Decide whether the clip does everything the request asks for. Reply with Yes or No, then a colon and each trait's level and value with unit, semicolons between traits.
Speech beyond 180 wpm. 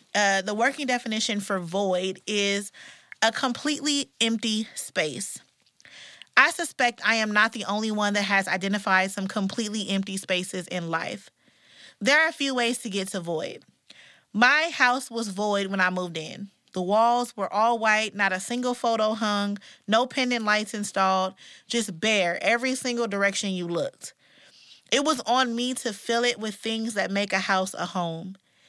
No: average, 170 wpm